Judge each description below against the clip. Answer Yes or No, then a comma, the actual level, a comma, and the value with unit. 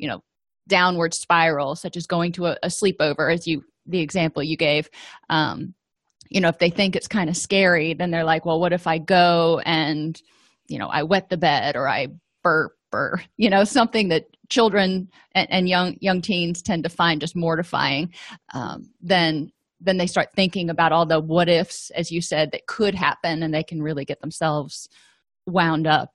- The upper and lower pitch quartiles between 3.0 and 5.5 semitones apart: No, narrow, 2.4 semitones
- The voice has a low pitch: No, medium, 170 Hz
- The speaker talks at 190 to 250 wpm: Yes, average, 195 wpm